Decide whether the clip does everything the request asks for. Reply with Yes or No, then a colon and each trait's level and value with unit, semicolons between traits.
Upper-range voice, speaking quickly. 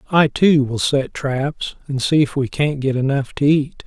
No: medium, 140 Hz; fast, 215 wpm